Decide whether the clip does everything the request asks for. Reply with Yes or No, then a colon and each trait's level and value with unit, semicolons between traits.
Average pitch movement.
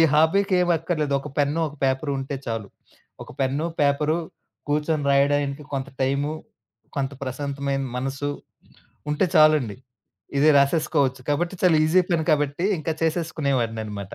No: narrow, 2.3 semitones